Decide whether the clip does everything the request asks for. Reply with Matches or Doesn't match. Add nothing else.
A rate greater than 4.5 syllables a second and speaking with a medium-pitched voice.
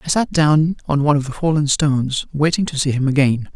Matches